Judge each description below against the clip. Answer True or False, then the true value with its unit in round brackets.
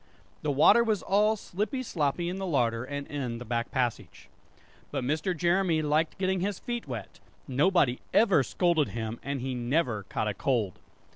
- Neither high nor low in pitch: True (150 Hz)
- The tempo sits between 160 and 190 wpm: True (170 wpm)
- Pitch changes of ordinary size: False (7.2 semitones)